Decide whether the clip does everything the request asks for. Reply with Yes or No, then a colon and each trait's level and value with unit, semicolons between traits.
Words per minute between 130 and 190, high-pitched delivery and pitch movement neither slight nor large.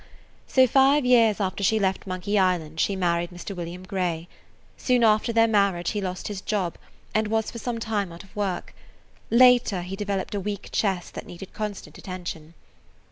Yes: average, 180 wpm; high, 200 Hz; average, 3.3 semitones